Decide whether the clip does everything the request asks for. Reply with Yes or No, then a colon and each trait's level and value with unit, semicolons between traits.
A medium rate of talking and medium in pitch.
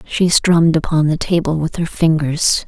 Yes: average, 180 wpm; medium, 160 Hz